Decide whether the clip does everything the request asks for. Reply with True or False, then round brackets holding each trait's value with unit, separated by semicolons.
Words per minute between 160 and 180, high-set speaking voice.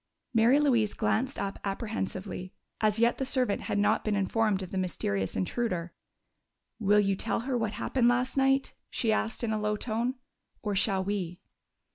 True (170 wpm; 215 Hz)